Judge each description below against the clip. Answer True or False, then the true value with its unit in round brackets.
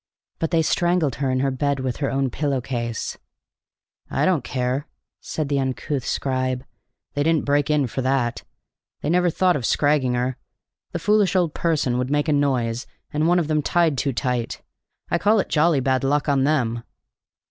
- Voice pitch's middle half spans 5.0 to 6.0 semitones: False (3.2 semitones)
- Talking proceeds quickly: False (185 wpm)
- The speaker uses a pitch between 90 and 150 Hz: True (140 Hz)